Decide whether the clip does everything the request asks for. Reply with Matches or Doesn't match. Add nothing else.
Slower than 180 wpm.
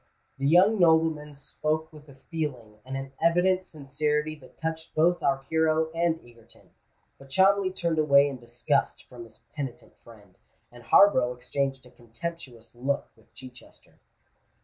Matches